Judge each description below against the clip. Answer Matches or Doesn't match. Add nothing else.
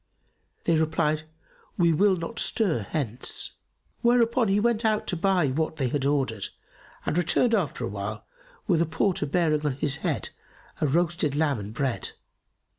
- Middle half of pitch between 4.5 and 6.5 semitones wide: Matches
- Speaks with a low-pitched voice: Doesn't match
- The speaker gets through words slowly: Doesn't match